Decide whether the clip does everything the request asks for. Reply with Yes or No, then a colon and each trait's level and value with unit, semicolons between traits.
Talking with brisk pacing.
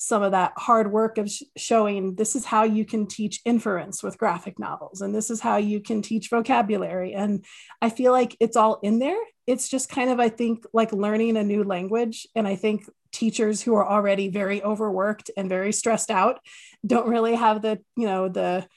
Yes: fast, 210 wpm